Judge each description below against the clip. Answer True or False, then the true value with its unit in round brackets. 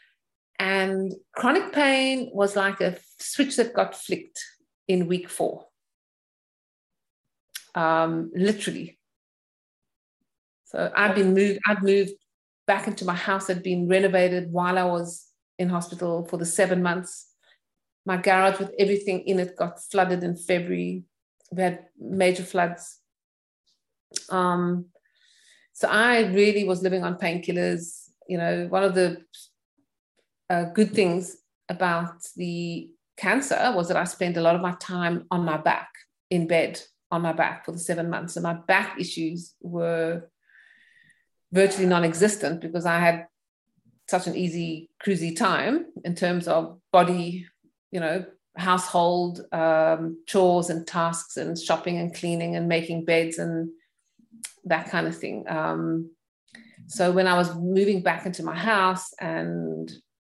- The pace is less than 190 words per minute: True (140 wpm)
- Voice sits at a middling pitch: True (180 Hz)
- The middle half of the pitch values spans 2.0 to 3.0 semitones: True (2.4 semitones)